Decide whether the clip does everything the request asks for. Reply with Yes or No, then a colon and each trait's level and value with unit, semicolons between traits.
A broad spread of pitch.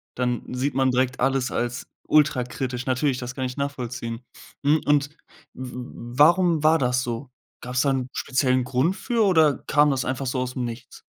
No: narrow, 2.5 semitones